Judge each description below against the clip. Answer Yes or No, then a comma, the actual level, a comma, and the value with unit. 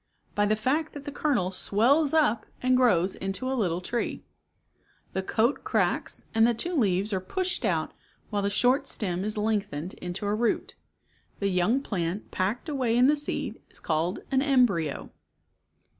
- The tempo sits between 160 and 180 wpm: Yes, average, 170 wpm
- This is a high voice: Yes, high, 215 Hz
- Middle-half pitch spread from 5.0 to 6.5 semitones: Yes, wide, 5.6 semitones